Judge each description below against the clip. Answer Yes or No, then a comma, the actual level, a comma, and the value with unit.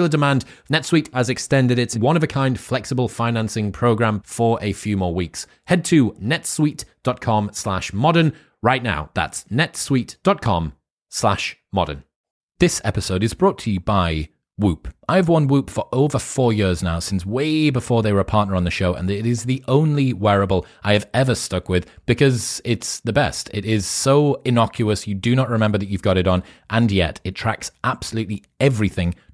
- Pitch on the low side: Yes, low, 115 Hz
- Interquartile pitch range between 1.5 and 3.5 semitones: No, average, 5.2 semitones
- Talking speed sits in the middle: Yes, average, 175 wpm